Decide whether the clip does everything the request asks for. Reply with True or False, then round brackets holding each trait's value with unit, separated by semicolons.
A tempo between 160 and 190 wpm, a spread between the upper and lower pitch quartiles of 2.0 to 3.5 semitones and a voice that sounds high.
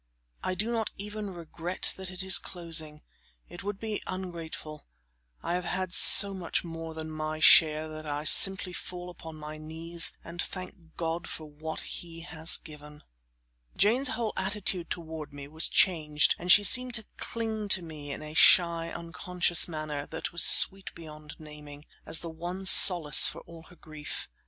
False (170 wpm; 3.1 semitones; 170 Hz)